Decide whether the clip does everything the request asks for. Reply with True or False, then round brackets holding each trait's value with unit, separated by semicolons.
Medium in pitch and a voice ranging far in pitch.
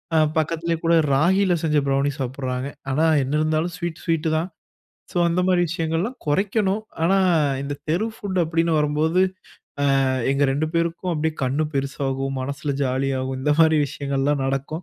False (155 Hz; 3.6 semitones)